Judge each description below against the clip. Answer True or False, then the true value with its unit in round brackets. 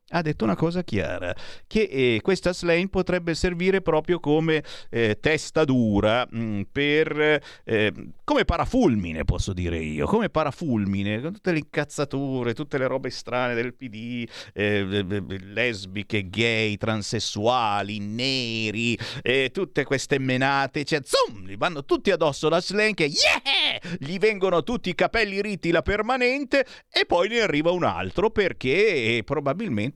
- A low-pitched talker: False (145 Hz)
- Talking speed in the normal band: True (145 wpm)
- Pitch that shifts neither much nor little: False (7.5 semitones)